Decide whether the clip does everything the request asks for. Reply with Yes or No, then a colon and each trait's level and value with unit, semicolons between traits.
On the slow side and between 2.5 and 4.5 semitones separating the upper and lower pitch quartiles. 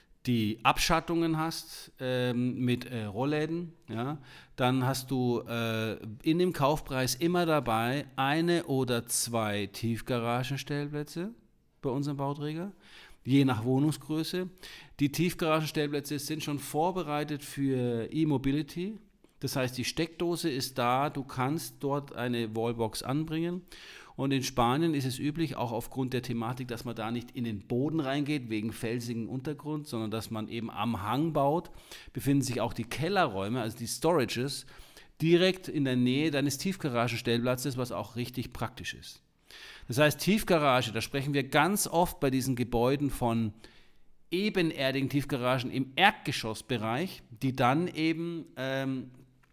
No: average, 135 wpm; average, 4.2 semitones